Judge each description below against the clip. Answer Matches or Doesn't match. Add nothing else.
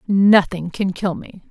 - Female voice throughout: Matches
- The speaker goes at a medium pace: Matches